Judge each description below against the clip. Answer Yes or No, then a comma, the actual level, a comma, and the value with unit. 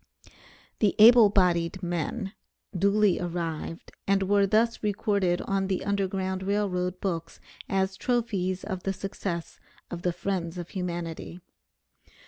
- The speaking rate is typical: No, slow, 125 wpm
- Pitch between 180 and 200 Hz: Yes, high, 190 Hz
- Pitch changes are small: Yes, narrow, 2.3 semitones